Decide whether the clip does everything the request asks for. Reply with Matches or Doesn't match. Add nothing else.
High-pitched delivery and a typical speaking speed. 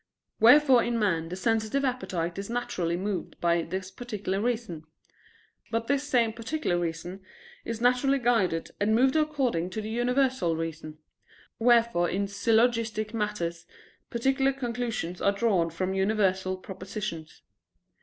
Doesn't match